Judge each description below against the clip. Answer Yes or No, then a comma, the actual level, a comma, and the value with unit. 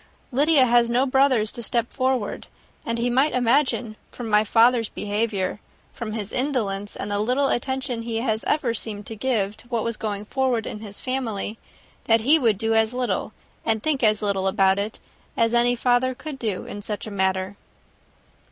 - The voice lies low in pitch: No, high, 230 Hz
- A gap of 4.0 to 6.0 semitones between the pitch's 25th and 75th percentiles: No, average, 3.3 semitones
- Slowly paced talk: No, average, 185 wpm